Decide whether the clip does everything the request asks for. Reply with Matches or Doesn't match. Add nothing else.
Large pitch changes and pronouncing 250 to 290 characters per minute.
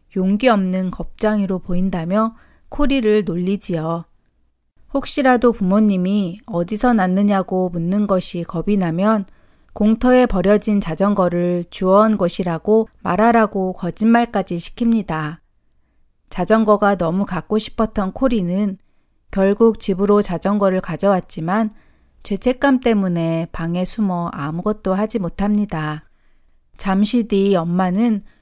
Doesn't match